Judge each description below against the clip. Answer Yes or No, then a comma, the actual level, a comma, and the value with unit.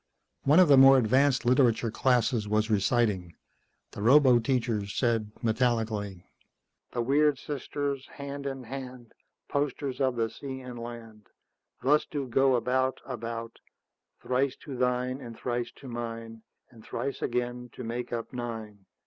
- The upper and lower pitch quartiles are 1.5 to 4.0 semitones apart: Yes, narrow, 2.6 semitones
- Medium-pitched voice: No, low, 125 Hz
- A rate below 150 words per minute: Yes, average, 140 wpm